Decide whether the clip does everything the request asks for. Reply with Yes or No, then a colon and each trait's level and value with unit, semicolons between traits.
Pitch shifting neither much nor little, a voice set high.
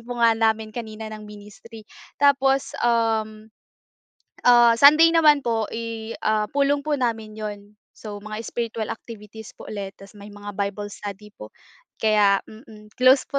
No: narrow, 2.1 semitones; high, 220 Hz